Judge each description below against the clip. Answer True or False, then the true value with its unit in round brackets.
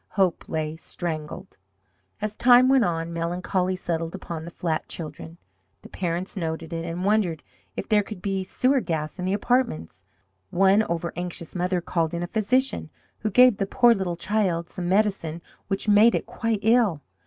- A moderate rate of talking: True (170 wpm)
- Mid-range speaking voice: True (180 Hz)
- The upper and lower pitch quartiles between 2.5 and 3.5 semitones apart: False (4.2 semitones)